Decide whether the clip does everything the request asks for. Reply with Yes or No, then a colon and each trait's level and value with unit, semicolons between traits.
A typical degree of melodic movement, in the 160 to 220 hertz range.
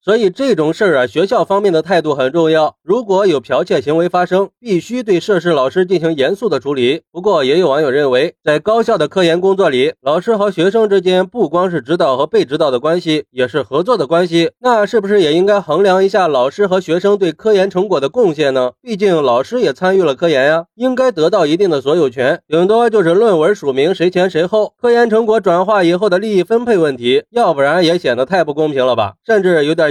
Yes: average, 4.9 semitones; medium, 185 Hz